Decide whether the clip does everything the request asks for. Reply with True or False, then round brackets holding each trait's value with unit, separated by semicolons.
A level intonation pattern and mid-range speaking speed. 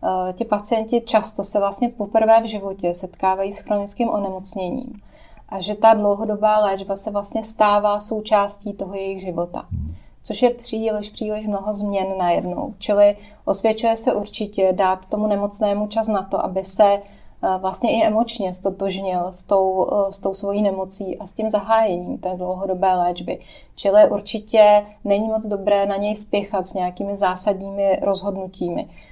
True (1.9 semitones; 150 wpm)